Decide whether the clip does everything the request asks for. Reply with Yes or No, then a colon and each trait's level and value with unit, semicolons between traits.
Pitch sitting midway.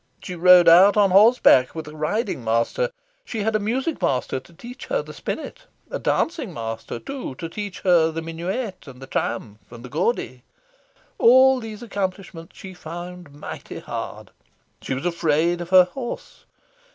Yes: medium, 180 Hz